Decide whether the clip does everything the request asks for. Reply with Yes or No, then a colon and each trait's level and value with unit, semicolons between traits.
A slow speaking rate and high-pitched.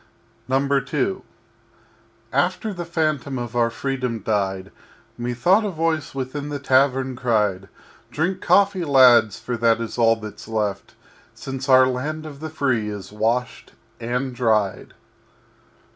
No: slow, 130 wpm; low, 130 Hz